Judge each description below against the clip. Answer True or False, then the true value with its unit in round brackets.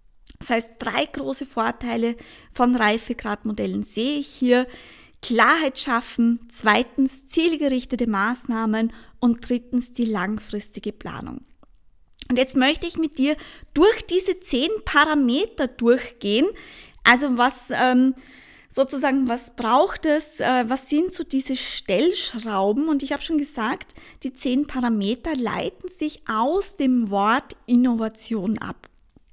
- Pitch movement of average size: True (3.8 semitones)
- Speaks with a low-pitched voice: False (255 Hz)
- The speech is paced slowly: True (115 wpm)